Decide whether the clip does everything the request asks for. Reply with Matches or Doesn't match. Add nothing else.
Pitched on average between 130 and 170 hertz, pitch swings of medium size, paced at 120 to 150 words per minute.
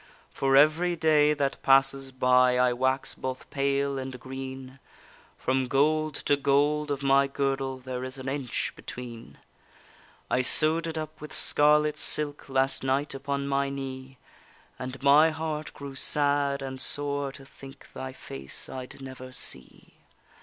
Doesn't match